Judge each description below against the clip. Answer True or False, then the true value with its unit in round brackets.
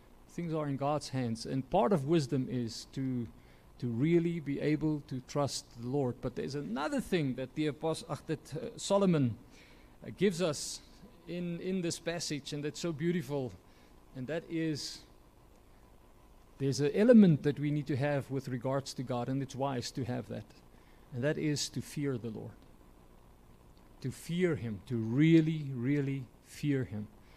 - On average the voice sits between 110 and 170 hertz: True (135 Hz)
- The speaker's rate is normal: True (170 wpm)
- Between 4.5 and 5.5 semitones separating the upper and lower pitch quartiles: True (5.1 semitones)